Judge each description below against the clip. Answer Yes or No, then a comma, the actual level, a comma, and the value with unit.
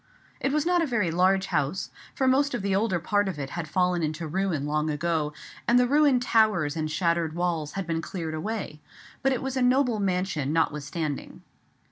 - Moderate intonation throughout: No, wide, 6.5 semitones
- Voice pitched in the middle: Yes, medium, 180 Hz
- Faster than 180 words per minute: Yes, average, 195 wpm